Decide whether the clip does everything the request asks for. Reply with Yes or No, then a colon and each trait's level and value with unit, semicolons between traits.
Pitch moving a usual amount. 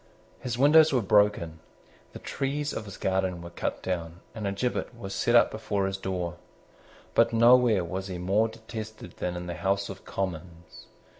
Yes: average, 4.2 semitones